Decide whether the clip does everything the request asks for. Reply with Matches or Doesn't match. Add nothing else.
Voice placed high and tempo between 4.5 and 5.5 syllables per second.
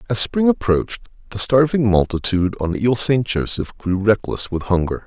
Doesn't match